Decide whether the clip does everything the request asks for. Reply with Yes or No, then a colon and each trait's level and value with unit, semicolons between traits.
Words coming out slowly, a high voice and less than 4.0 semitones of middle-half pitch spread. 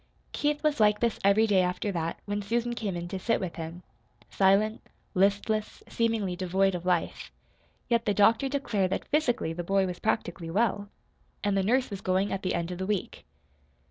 No: average, 190 wpm; high, 200 Hz; average, 3.4 semitones